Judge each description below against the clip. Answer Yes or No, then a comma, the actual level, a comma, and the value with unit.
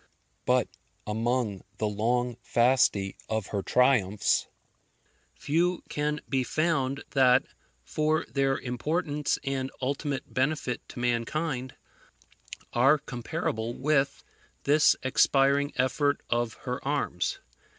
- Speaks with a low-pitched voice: Yes, low, 130 Hz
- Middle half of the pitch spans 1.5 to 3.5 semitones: Yes, average, 3.2 semitones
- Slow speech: Yes, slow, 100 wpm